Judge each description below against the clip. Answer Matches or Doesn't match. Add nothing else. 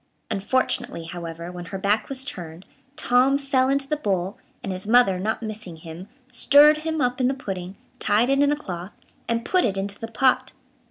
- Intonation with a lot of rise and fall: Matches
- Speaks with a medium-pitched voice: Doesn't match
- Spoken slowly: Doesn't match